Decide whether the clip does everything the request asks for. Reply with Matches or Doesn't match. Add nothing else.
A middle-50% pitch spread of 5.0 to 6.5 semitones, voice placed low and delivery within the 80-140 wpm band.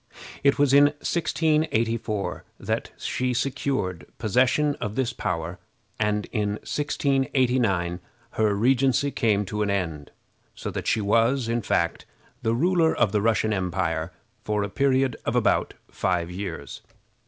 Matches